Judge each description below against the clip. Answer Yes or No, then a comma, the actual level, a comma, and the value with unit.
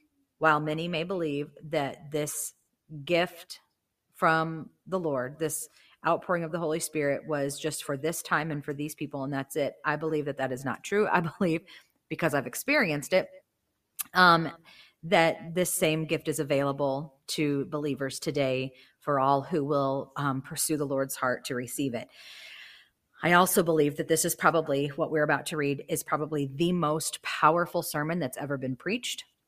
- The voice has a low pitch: No, medium, 155 Hz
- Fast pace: No, average, 175 wpm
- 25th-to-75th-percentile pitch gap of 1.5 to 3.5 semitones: Yes, average, 2.7 semitones